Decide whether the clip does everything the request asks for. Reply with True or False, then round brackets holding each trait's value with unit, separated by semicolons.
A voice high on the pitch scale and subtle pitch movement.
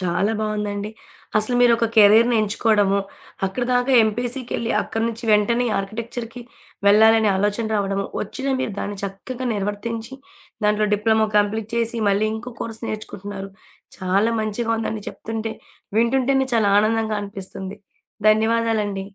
True (220 Hz; 2.1 semitones)